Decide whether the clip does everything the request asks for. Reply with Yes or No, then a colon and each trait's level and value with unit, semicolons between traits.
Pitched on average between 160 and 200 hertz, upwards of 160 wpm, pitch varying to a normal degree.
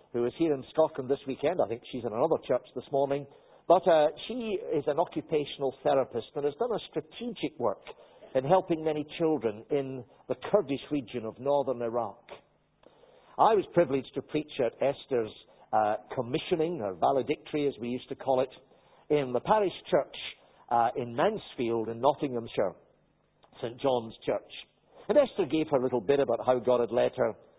No: medium, 140 Hz; average, 175 wpm; average, 4.0 semitones